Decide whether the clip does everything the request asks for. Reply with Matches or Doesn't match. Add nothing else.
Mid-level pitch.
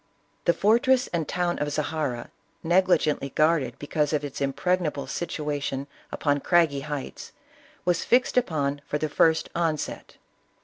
Matches